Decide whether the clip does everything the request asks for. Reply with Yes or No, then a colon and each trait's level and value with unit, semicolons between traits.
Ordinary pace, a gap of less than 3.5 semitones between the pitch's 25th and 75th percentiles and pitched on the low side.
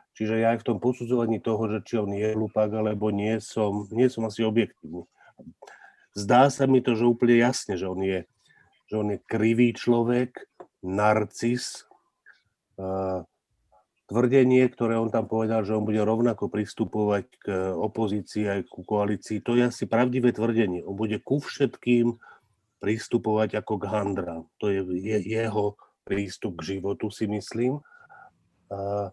Yes: average, 145 wpm; narrow, 2.5 semitones; low, 110 Hz